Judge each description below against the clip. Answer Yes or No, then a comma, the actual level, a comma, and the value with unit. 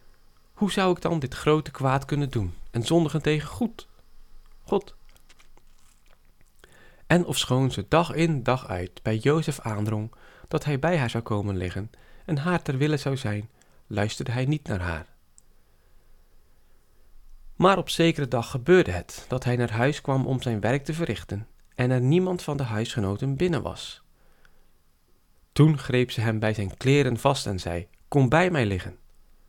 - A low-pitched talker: Yes, low, 120 Hz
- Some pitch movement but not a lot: No, wide, 8.1 semitones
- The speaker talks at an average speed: Yes, average, 165 wpm